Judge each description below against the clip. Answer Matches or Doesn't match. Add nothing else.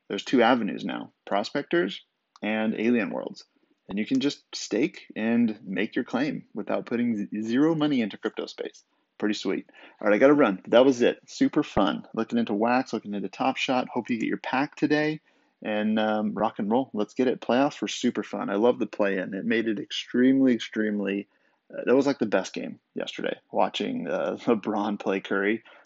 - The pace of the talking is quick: Doesn't match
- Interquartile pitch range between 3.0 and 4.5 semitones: Matches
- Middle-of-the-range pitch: Doesn't match